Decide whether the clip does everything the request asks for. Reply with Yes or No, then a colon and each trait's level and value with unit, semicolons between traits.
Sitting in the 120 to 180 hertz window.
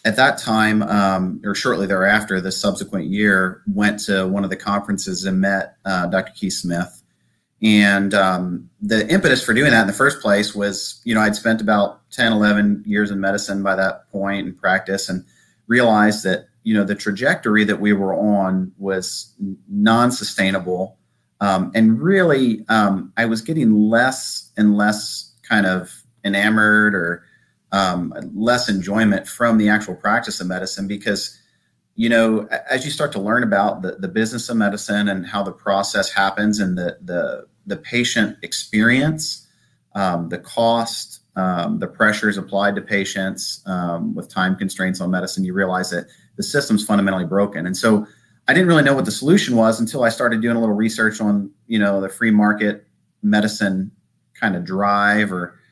No: low, 105 Hz